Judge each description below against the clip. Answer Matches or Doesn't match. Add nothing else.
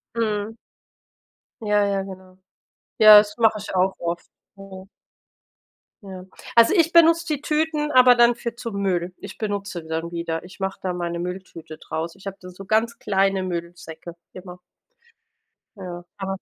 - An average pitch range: Matches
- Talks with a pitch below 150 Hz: Doesn't match